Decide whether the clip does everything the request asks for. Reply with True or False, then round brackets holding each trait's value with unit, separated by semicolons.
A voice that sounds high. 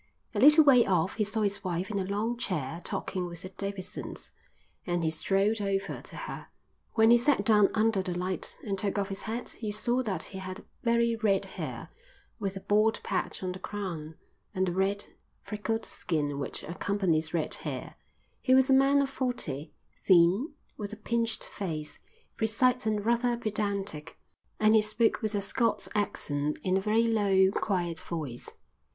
True (200 Hz)